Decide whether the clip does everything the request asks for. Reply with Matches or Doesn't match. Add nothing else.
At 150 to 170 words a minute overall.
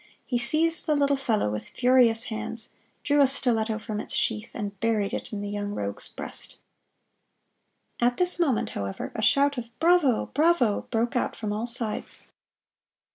Matches